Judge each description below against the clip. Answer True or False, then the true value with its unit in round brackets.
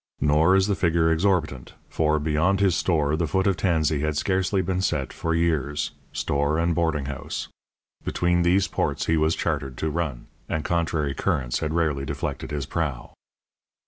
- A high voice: False (80 Hz)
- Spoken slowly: False (170 wpm)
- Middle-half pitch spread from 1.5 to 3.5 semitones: True (2.8 semitones)